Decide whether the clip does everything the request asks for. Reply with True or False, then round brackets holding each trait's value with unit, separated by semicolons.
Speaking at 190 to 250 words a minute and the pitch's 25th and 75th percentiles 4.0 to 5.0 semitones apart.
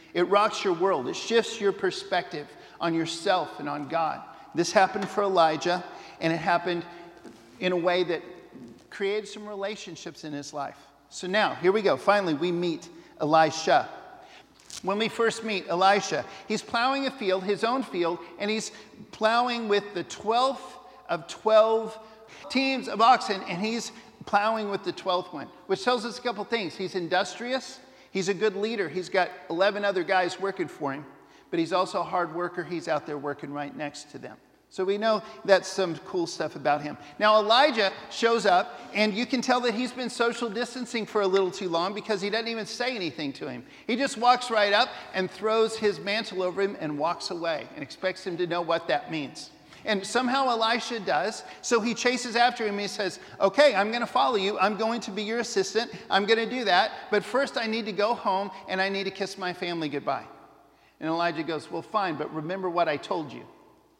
True (200 wpm; 4.4 semitones)